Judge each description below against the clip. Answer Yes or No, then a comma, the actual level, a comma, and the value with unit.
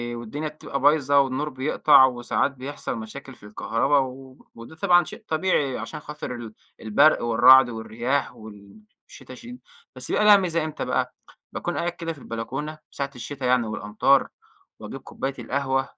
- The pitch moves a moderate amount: Yes, average, 4.0 semitones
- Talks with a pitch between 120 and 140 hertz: Yes, low, 135 Hz